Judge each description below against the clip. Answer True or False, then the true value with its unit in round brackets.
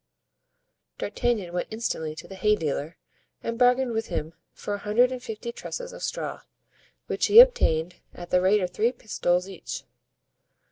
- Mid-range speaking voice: False (210 Hz)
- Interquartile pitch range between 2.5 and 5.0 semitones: False (5.4 semitones)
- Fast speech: False (160 wpm)